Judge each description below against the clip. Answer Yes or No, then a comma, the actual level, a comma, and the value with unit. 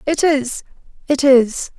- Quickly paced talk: No, slow, 100 wpm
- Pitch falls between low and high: No, very high, 270 Hz